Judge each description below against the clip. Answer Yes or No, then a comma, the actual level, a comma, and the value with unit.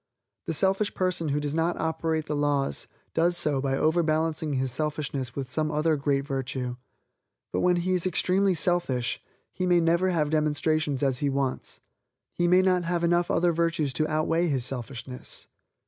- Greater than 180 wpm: No, average, 165 wpm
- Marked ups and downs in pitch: No, average, 3.7 semitones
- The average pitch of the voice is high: No, medium, 155 Hz